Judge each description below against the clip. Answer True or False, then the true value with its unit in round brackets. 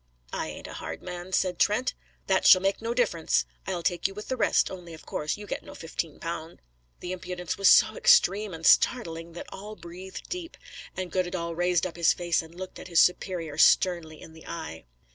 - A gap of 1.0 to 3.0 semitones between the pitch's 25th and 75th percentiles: True (2.6 semitones)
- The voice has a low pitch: False (180 Hz)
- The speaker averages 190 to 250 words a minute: True (200 wpm)